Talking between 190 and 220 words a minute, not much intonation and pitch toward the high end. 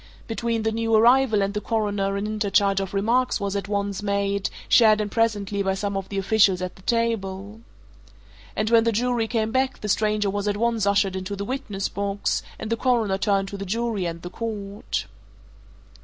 Yes: average, 195 wpm; narrow, 2.3 semitones; high, 205 Hz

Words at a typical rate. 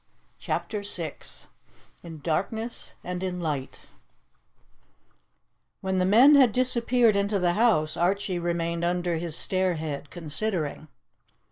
No: slow, 110 wpm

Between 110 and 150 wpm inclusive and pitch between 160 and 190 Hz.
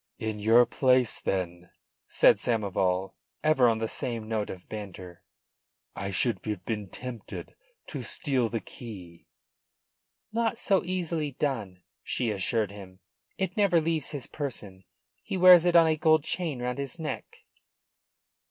No: average, 145 wpm; low, 120 Hz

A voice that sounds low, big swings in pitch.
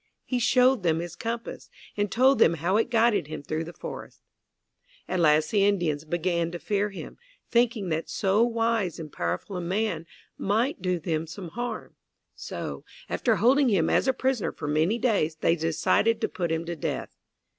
No: high, 190 Hz; wide, 5.8 semitones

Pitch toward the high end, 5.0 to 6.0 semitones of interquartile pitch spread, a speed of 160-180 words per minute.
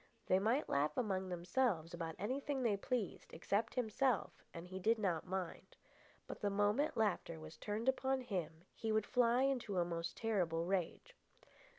Yes: high, 205 Hz; wide, 5.5 semitones; average, 165 wpm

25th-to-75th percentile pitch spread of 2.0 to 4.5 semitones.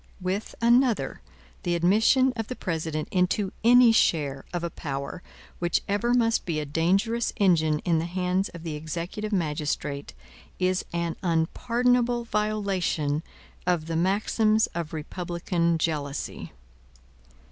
No: average, 4.9 semitones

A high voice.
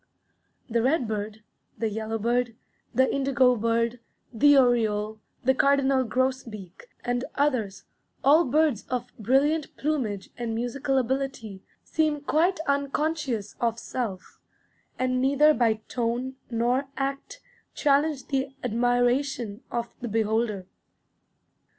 Yes: very high, 250 Hz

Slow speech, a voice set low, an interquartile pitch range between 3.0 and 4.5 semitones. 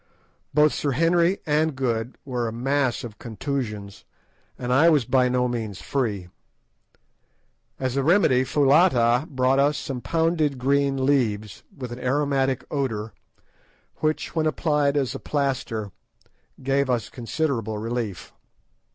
Yes: slow, 130 wpm; low, 130 Hz; average, 3.3 semitones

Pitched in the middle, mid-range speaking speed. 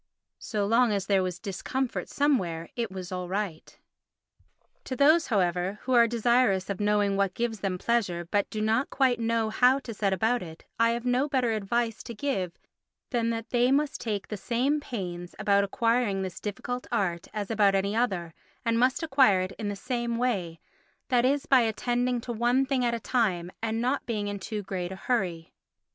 No: high, 225 Hz; average, 190 wpm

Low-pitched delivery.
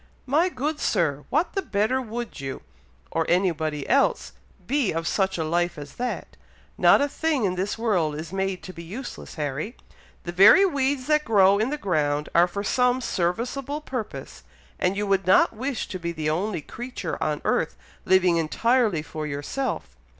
No: high, 195 Hz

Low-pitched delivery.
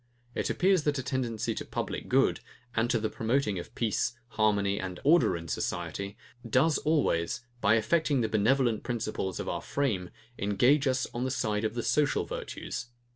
Yes: low, 115 Hz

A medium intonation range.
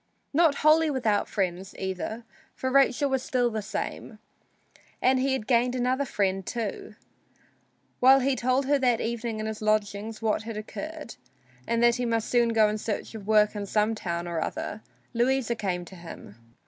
Yes: average, 3.5 semitones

